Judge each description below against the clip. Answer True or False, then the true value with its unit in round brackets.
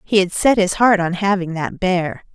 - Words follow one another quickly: True (230 wpm)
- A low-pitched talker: False (185 Hz)